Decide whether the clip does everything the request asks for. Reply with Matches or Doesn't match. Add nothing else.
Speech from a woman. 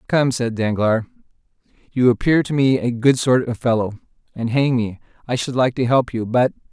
Doesn't match